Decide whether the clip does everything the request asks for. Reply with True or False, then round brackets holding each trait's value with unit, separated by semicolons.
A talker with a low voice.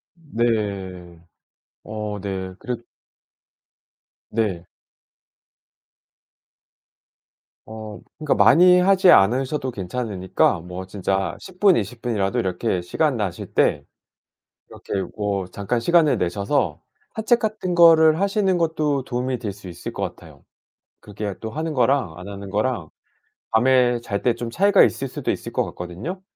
True (115 Hz)